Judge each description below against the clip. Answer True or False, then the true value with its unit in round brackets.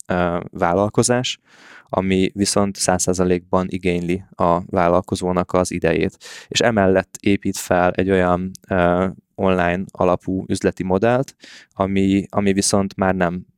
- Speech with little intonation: True (1.6 semitones)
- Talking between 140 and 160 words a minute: False (115 wpm)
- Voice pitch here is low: True (95 Hz)